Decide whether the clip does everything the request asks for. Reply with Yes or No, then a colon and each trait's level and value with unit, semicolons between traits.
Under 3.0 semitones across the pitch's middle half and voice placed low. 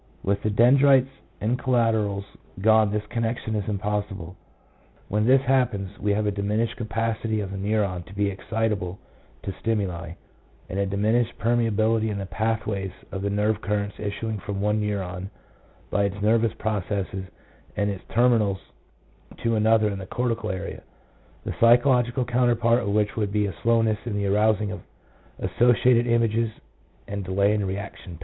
Yes: narrow, 2.4 semitones; low, 105 Hz